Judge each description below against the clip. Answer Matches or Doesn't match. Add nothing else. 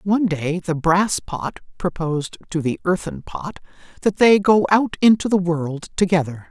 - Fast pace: Doesn't match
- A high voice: Doesn't match